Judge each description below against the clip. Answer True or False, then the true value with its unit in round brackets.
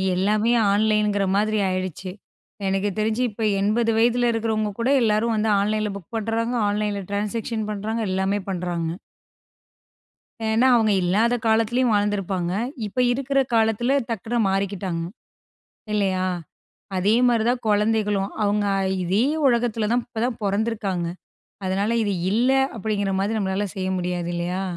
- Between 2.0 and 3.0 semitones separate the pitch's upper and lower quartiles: True (2.6 semitones)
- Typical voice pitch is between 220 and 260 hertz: False (210 Hz)